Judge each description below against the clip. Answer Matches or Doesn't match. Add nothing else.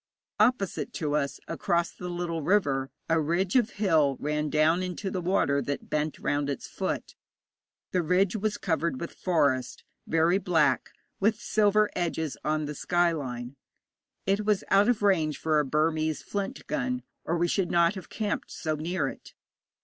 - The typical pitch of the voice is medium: Matches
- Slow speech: Doesn't match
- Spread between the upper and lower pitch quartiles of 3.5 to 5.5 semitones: Matches